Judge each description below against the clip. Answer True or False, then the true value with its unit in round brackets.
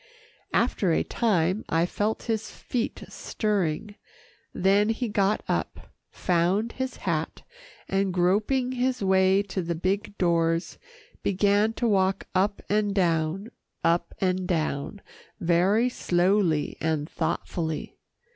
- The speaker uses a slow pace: True (120 wpm)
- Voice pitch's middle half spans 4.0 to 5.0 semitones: False (3.4 semitones)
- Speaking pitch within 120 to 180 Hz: False (195 Hz)